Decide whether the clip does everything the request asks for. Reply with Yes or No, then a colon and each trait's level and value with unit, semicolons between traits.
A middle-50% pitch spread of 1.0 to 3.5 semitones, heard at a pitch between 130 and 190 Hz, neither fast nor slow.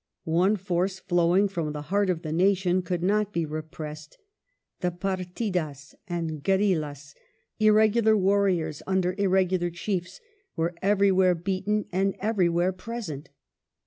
No: average, 2.8 semitones; medium, 185 Hz; slow, 120 wpm